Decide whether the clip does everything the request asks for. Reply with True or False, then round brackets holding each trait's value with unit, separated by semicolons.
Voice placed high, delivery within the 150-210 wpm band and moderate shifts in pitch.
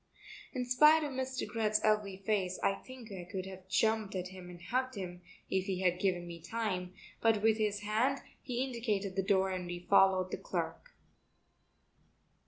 True (200 Hz; 180 wpm; 3.7 semitones)